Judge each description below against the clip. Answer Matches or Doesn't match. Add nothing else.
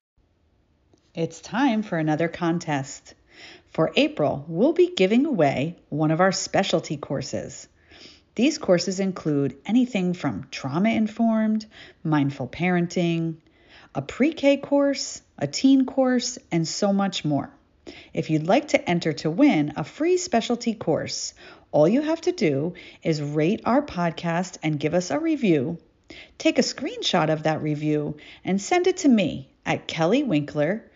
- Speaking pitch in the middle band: Matches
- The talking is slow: Doesn't match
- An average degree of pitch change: Doesn't match